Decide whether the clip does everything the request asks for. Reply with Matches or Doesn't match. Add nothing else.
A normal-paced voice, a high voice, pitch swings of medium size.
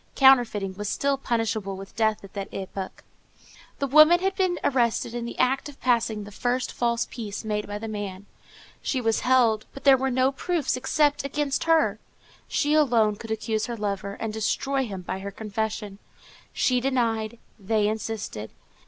Matches